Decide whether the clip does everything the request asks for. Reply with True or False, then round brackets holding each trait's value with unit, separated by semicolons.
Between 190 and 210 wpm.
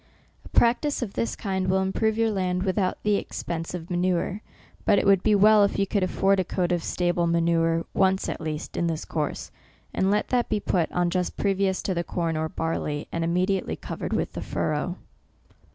True (200 wpm)